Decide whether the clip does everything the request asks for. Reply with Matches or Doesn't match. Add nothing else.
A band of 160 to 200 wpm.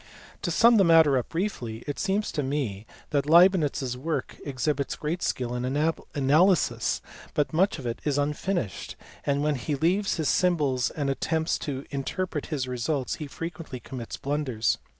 Matches